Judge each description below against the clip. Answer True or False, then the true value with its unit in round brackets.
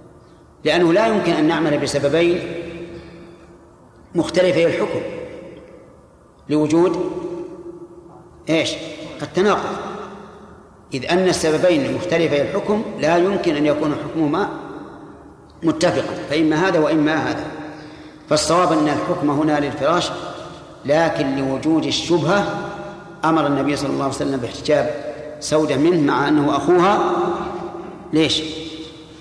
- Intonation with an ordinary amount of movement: True (3.3 semitones)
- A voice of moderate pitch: True (160 Hz)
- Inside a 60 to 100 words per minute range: True (95 wpm)